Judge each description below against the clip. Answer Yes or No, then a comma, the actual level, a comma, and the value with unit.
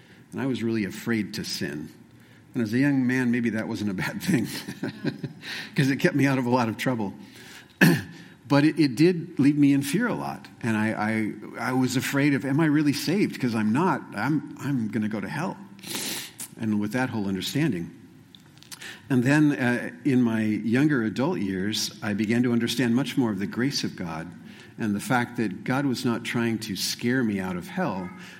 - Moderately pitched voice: No, low, 120 Hz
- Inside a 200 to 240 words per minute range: Yes, fast, 205 wpm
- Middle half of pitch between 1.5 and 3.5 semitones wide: No, average, 4.0 semitones